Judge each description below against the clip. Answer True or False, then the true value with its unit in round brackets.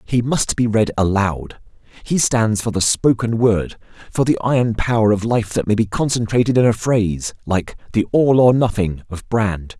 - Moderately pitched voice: False (110 Hz)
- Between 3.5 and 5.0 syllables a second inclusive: True (4.7 syllables/s)